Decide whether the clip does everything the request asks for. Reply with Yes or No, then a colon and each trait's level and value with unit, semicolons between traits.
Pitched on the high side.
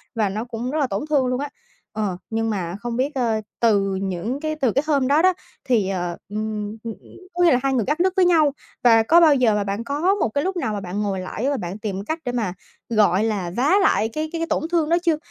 Yes: high, 235 Hz